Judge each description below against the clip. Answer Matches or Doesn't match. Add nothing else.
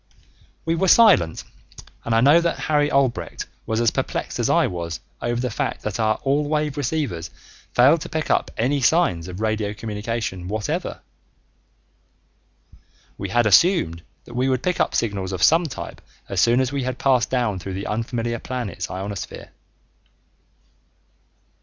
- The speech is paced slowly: Doesn't match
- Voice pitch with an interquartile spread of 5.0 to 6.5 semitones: Matches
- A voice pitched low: Matches